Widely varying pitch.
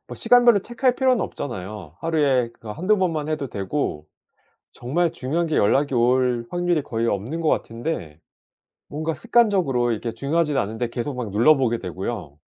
Yes: wide, 6.2 semitones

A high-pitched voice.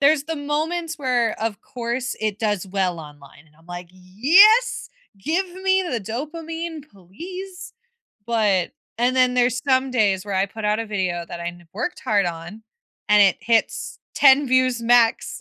Yes: high, 235 Hz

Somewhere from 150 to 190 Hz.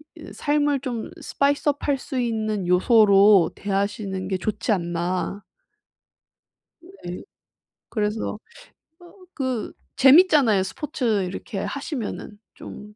No: high, 215 Hz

